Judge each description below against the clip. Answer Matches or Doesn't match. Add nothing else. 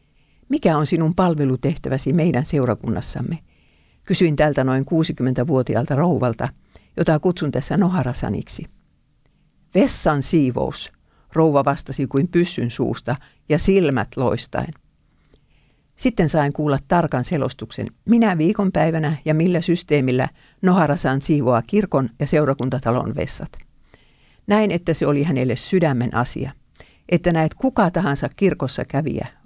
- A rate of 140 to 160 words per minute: Doesn't match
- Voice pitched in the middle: Matches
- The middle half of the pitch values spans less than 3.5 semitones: Doesn't match